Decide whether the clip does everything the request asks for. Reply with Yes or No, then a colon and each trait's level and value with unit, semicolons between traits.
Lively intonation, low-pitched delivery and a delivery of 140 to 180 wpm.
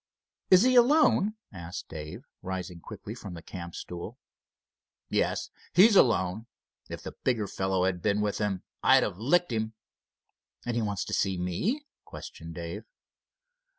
Yes: wide, 5.8 semitones; low, 100 Hz; average, 150 wpm